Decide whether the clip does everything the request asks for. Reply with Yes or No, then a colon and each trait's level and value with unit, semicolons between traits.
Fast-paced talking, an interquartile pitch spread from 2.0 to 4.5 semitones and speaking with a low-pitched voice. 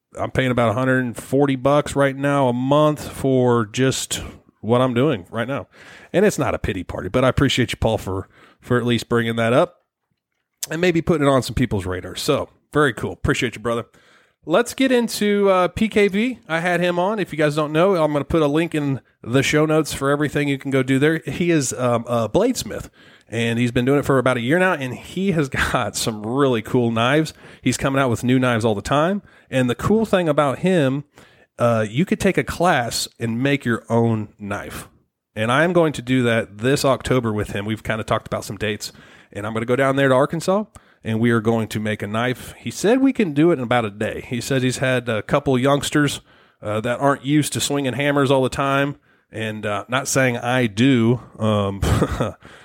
Yes: fast, 225 wpm; average, 4.2 semitones; low, 130 Hz